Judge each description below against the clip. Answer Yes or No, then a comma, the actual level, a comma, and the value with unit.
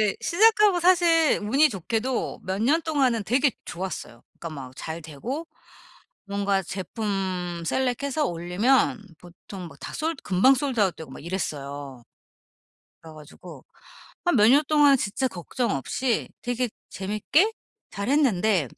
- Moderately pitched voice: No, high, 215 Hz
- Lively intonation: Yes, wide, 7.5 semitones